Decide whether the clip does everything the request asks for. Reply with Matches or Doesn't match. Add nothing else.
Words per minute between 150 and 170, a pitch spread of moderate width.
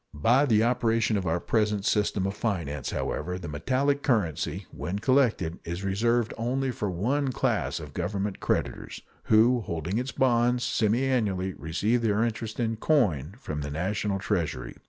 Matches